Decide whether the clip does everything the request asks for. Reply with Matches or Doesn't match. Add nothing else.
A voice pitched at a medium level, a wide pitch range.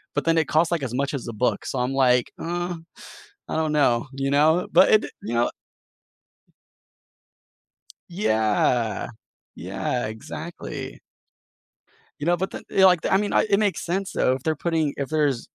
Matches